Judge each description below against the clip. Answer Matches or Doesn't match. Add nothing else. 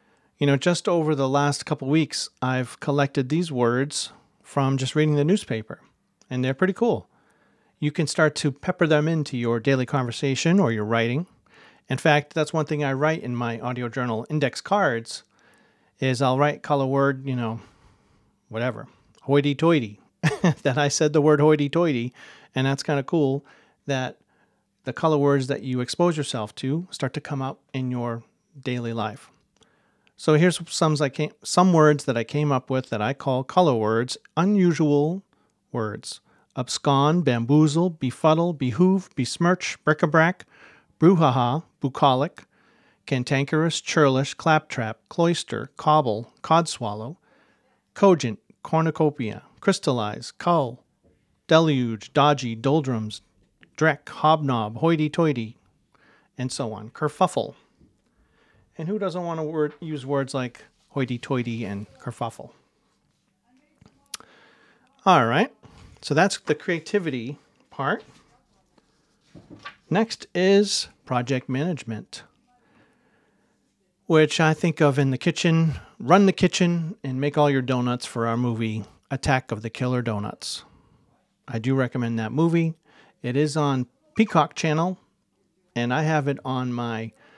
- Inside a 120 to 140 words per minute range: Matches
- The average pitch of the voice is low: Doesn't match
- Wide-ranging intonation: Doesn't match